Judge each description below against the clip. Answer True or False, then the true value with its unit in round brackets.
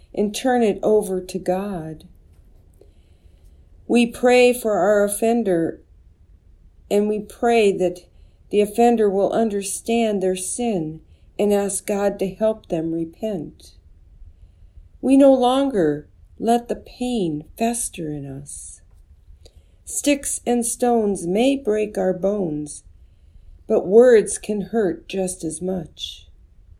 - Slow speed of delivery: True (115 wpm)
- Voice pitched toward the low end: False (185 Hz)